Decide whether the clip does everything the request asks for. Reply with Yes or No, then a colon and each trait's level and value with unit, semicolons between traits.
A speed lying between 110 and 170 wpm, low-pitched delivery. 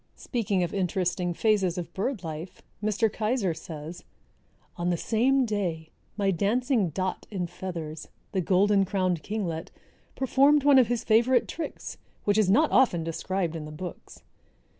No: average, 150 wpm; high, 190 Hz